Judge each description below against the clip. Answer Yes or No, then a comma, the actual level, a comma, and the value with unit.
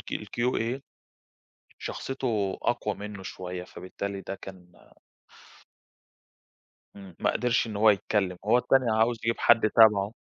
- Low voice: Yes, low, 105 Hz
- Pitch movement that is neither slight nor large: Yes, average, 3.3 semitones